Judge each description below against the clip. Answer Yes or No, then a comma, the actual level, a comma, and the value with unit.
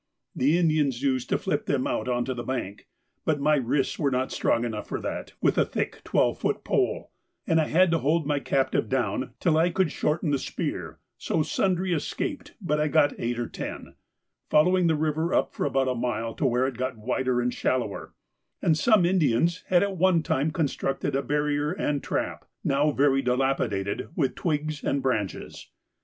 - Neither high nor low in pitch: Yes, medium, 145 Hz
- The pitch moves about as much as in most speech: Yes, average, 3.8 semitones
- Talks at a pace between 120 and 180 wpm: No, average, 190 wpm